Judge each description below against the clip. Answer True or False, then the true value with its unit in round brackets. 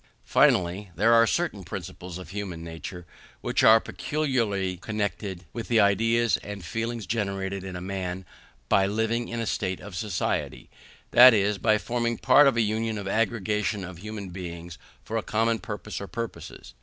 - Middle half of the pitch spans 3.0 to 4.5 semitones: True (3.4 semitones)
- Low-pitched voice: True (105 Hz)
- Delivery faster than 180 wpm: False (165 wpm)